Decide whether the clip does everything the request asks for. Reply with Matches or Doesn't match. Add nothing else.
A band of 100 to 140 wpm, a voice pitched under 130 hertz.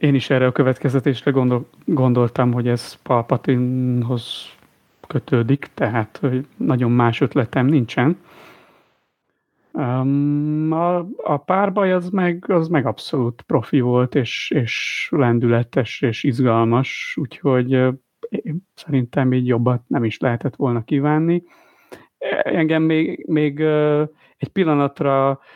Doesn't match